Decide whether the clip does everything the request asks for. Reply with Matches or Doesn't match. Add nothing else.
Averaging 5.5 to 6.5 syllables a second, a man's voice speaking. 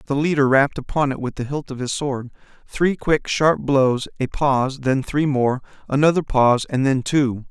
Doesn't match